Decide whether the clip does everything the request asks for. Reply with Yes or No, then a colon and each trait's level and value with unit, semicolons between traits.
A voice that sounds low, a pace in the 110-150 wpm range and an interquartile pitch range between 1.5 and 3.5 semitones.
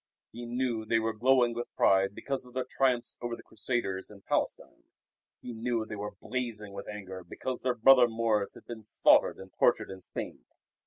No: low, 115 Hz; average, 190 wpm; average, 2.9 semitones